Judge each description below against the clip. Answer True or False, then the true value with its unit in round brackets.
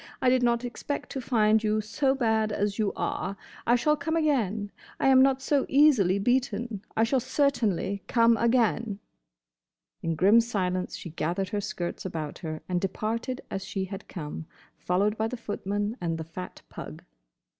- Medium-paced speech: True (170 wpm)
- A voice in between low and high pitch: False (215 Hz)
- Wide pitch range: False (4.3 semitones)